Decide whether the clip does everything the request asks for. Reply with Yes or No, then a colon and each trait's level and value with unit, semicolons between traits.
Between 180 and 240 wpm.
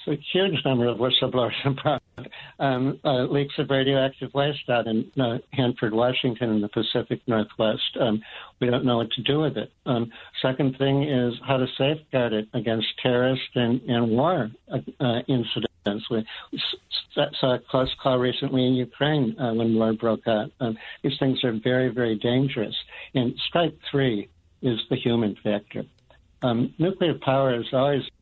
No: average, 165 wpm